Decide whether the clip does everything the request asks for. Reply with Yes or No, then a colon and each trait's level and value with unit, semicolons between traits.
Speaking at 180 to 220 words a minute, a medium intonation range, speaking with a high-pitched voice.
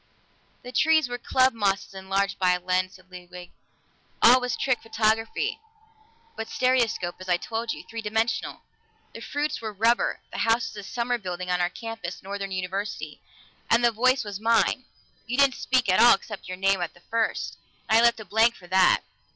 Yes: average, 190 wpm; average, 4.1 semitones; high, 220 Hz